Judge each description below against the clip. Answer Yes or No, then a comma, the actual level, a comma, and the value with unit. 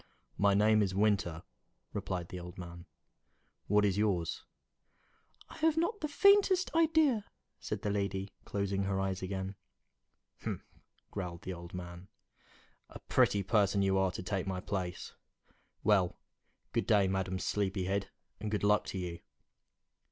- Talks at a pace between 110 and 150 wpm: Yes, average, 145 wpm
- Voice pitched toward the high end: No, low, 100 Hz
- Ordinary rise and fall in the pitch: No, narrow, 2.2 semitones